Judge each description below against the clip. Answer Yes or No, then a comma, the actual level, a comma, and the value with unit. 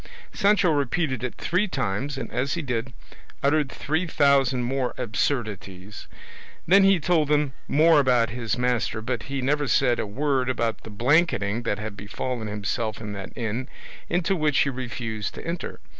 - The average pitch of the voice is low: Yes, low, 130 Hz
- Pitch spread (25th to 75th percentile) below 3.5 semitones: No, average, 4.8 semitones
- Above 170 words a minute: No, average, 165 wpm